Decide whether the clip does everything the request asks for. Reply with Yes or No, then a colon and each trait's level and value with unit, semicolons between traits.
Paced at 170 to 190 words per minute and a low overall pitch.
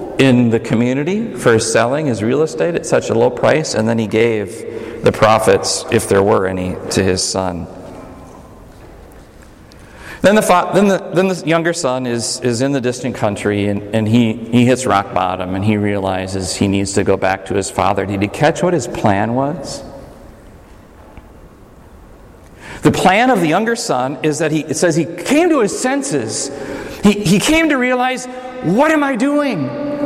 Yes: average, 180 wpm; low, 125 Hz